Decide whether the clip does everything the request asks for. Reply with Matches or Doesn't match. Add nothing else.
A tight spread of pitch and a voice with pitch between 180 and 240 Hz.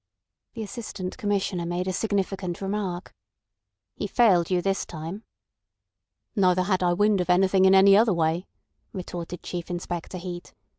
Matches